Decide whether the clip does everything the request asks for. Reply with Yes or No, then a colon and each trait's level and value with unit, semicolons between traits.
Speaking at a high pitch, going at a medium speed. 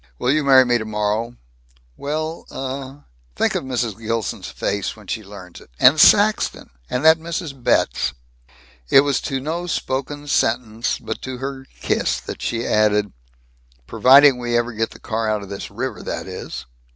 No: low, 125 Hz; average, 170 wpm